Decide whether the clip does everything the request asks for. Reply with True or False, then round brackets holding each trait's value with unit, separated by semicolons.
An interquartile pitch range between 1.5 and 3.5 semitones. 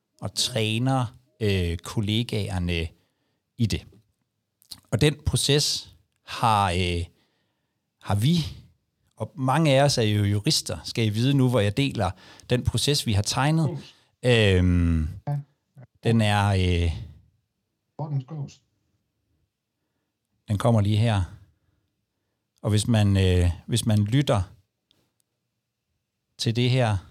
False (3.9 semitones)